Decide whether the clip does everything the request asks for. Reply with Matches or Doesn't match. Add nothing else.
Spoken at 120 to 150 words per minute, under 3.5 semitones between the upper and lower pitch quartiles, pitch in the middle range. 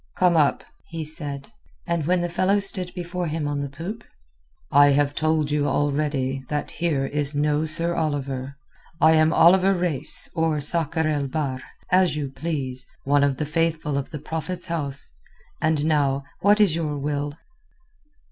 Doesn't match